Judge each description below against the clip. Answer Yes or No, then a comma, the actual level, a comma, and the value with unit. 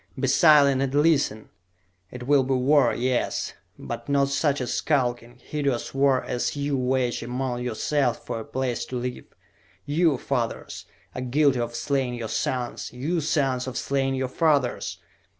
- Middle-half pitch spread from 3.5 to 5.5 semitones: No, narrow, 2.4 semitones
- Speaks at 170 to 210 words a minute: No, average, 155 wpm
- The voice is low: Yes, low, 130 Hz